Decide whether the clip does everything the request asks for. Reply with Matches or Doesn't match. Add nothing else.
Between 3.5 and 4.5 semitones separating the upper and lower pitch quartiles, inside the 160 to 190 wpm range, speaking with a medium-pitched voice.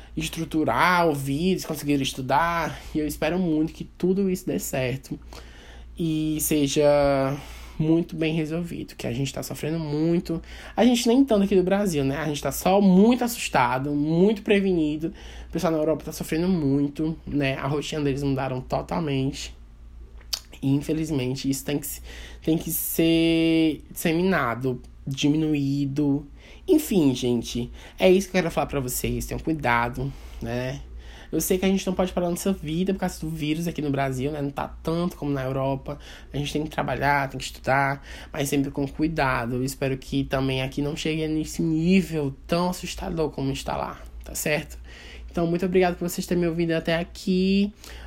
Matches